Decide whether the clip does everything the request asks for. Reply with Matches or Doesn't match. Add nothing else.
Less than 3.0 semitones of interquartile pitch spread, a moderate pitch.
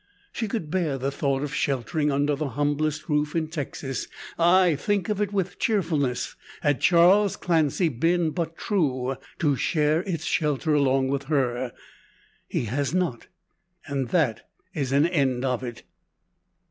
Doesn't match